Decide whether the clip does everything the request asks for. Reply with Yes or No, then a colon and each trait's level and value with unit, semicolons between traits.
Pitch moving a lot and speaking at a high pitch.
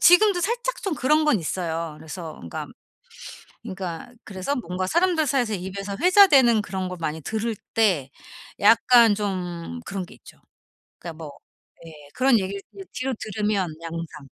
Yes: wide, 7.1 semitones; high, 200 Hz